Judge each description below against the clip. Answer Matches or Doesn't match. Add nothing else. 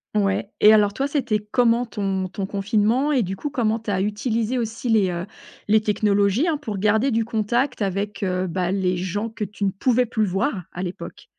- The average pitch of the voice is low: Doesn't match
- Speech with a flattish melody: Doesn't match